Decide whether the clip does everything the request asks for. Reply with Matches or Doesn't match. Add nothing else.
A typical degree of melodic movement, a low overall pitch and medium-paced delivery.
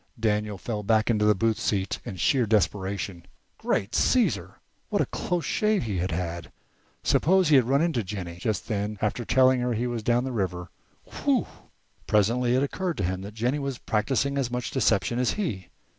Matches